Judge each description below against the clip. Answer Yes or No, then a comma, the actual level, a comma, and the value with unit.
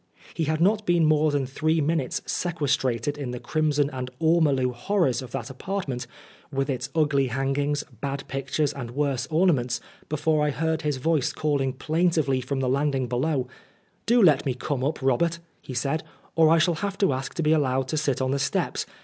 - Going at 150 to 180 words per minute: No, fast, 205 wpm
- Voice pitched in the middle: Yes, medium, 145 Hz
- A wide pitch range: No, average, 3.2 semitones